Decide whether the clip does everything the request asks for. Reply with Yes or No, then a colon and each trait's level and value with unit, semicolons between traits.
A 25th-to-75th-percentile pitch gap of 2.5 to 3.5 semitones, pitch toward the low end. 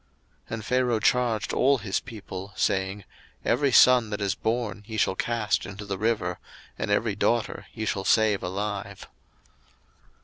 Yes: average, 2.9 semitones; low, 105 Hz